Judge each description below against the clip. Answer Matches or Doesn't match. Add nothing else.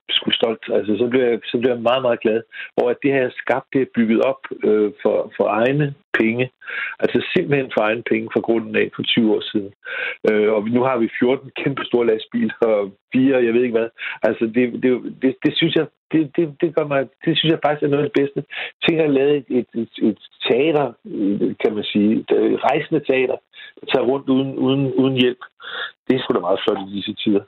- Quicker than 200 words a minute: Matches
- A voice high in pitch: Doesn't match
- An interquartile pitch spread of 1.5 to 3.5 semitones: Doesn't match